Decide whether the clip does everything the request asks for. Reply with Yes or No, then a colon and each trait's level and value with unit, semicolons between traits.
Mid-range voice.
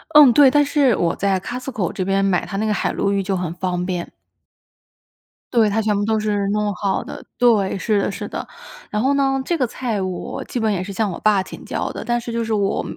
No: high, 210 Hz